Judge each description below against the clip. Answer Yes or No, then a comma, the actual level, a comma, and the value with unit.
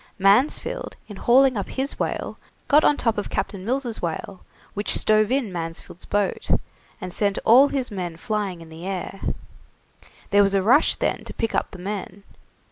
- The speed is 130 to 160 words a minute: No, average, 175 wpm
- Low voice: No, high, 205 Hz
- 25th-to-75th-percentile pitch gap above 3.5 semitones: Yes, average, 4.2 semitones